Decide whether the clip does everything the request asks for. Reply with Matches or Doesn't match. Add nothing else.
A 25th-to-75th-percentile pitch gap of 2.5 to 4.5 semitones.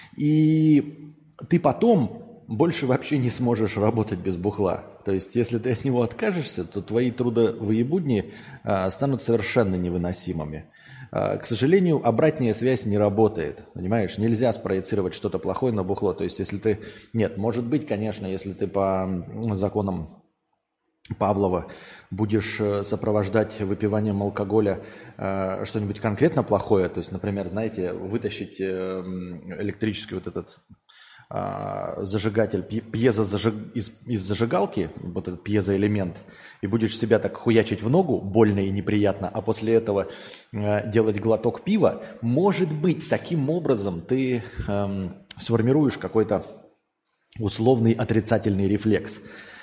Matches